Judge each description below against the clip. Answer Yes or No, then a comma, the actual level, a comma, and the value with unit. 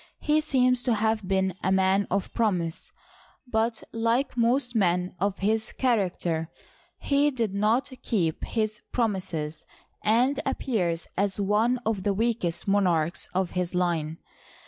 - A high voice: Yes, high, 205 Hz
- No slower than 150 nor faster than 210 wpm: No, slow, 135 wpm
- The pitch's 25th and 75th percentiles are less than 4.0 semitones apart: No, average, 4.4 semitones